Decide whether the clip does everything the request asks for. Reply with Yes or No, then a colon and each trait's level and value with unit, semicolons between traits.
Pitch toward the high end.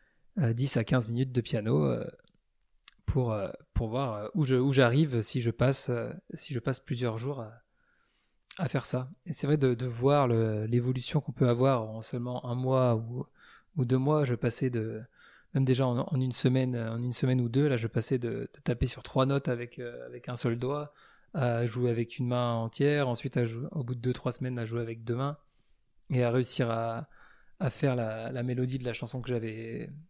No: low, 125 Hz